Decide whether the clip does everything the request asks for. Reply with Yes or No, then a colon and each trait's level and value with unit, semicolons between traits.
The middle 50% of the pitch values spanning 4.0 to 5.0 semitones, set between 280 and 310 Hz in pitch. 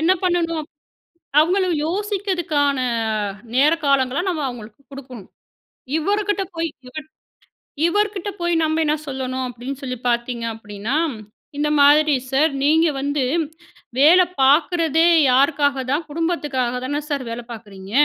Yes: average, 4.4 semitones; very high, 290 Hz